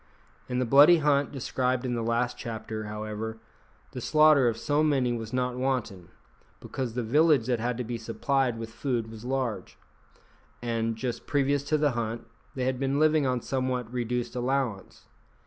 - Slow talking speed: No, average, 170 wpm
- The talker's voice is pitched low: Yes, low, 125 Hz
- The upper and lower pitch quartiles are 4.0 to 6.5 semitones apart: No, average, 2.9 semitones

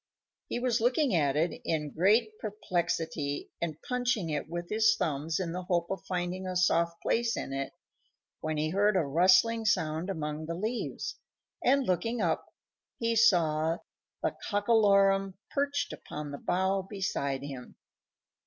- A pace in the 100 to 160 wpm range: Yes, average, 150 wpm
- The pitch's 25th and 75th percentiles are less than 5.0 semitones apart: No, average, 5.3 semitones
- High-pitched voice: No, medium, 180 Hz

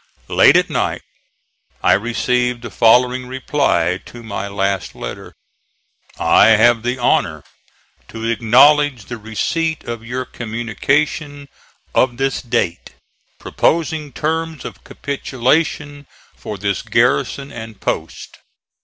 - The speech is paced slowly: Yes, slow, 110 wpm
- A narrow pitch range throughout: No, average, 4.1 semitones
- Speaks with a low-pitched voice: Yes, low, 125 Hz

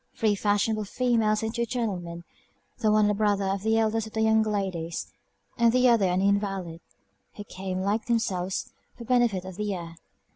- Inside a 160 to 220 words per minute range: Yes, average, 185 wpm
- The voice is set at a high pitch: Yes, high, 210 Hz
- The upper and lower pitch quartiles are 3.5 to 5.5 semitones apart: No, average, 2.8 semitones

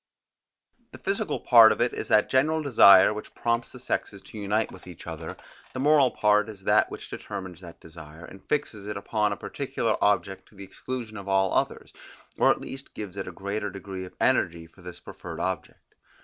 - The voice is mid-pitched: No, low, 100 Hz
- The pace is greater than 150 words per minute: Yes, average, 200 wpm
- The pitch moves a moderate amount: Yes, average, 3.3 semitones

